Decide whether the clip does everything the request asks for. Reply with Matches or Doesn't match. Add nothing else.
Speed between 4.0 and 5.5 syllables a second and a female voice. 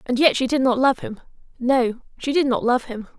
Matches